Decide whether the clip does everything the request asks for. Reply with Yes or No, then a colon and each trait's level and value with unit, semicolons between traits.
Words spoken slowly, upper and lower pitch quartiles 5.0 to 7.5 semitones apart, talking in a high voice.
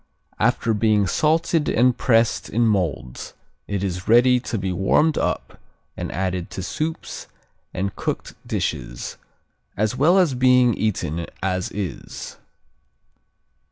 No: slow, 125 wpm; wide, 5.4 semitones; low, 110 Hz